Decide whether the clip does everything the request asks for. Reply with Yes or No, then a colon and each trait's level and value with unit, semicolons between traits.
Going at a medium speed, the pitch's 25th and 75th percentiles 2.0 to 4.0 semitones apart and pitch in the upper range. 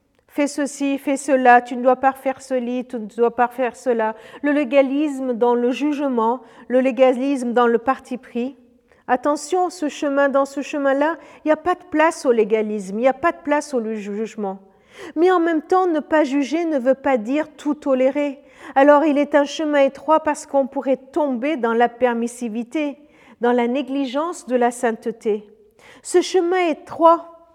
Yes: average, 185 wpm; average, 3.4 semitones; very high, 270 Hz